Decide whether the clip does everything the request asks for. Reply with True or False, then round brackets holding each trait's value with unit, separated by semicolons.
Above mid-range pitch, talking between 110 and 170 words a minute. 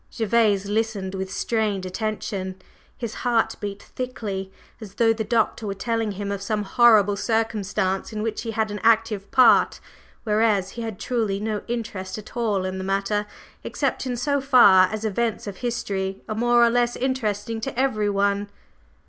True (215 Hz; 165 wpm)